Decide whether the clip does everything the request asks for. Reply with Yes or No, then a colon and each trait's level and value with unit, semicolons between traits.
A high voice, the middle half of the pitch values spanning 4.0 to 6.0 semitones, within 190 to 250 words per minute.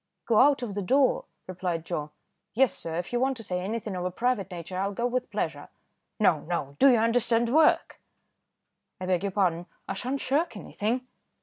Yes: high, 210 Hz; wide, 5.4 semitones; average, 195 wpm